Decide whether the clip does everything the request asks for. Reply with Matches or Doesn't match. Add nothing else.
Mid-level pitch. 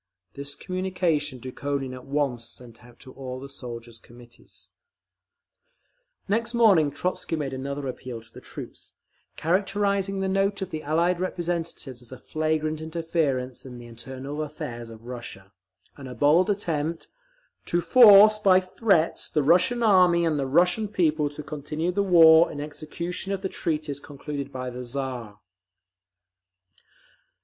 Matches